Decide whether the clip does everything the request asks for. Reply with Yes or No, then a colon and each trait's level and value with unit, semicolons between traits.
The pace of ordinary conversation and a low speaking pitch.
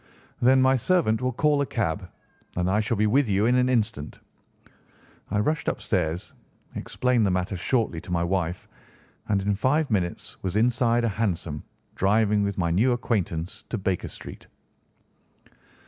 Yes: average, 160 wpm; low, 105 Hz